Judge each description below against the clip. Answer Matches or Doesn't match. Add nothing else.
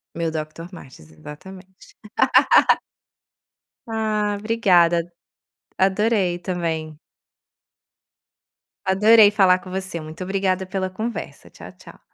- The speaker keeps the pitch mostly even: Doesn't match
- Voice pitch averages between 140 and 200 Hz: Matches